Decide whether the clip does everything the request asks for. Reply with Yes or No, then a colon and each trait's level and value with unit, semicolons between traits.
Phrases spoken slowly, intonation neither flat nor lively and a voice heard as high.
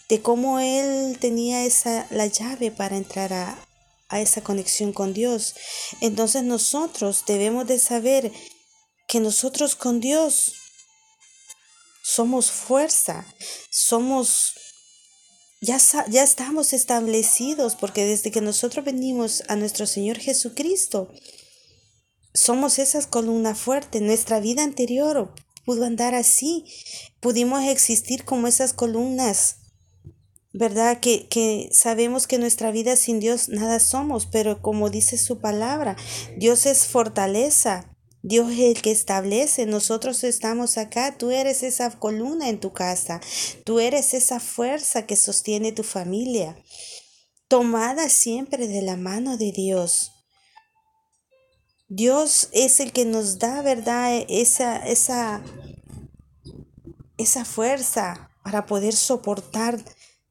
Yes: slow, 120 wpm; average, 3.4 semitones; high, 235 Hz